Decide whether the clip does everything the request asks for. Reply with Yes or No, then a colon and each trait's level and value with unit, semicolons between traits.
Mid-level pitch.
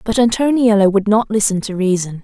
No: high, 210 Hz